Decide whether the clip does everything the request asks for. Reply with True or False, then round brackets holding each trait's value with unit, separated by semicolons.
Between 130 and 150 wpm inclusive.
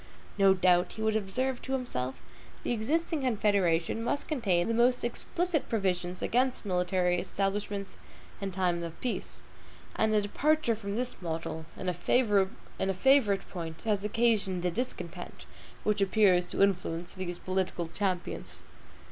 True (140 wpm)